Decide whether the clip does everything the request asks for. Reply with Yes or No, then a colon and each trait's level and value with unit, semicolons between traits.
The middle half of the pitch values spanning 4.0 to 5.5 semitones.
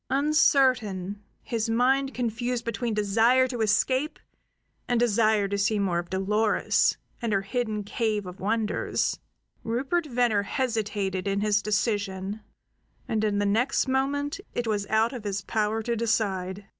No: average, 3.2 semitones